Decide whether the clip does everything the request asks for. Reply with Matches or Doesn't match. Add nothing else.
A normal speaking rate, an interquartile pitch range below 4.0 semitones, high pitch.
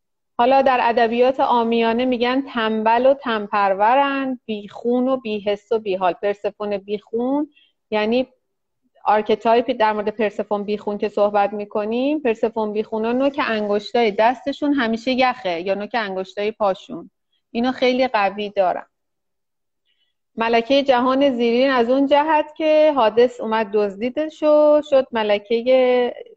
Matches